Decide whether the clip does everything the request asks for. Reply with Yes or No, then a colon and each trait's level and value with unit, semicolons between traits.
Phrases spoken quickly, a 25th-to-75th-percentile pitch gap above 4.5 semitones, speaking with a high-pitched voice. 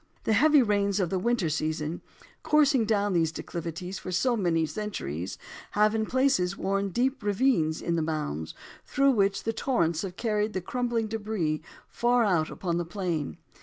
No: average, 165 wpm; average, 5.1 semitones; high, 200 Hz